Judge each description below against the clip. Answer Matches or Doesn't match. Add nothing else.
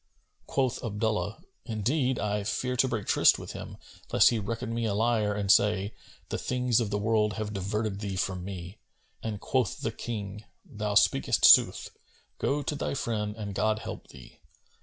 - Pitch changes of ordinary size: Doesn't match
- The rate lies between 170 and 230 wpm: Matches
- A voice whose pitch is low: Matches